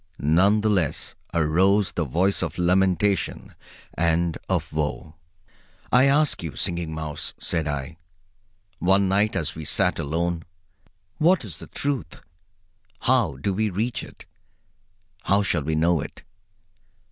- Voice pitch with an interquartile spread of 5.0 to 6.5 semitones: No, average, 4.1 semitones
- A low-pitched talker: Yes, very low, 85 Hz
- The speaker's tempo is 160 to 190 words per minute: No, slow, 135 wpm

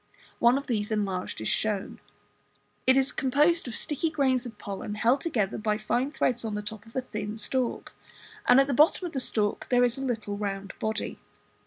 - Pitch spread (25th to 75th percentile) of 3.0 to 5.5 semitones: Yes, average, 4.1 semitones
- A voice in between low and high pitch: No, high, 235 Hz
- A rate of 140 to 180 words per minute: No, average, 200 wpm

